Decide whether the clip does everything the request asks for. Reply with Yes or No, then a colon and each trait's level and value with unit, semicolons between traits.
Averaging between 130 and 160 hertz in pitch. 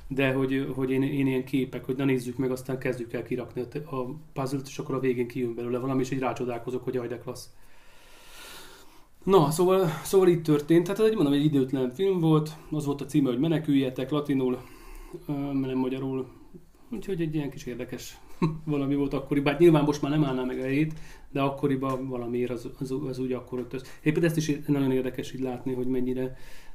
Yes: low, 135 Hz